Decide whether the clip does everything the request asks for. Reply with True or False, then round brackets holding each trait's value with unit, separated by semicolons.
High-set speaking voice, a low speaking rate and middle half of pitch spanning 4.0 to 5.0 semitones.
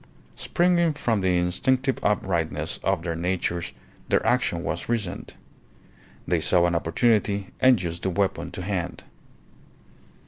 False (95 Hz; 130 wpm; 4.5 semitones)